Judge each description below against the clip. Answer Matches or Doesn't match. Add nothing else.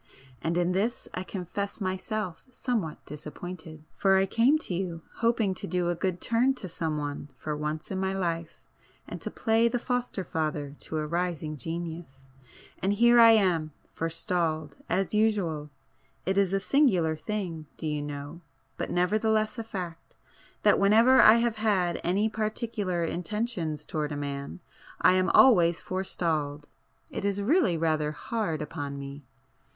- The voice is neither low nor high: Matches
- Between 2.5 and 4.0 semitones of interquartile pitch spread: Doesn't match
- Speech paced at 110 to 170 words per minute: Matches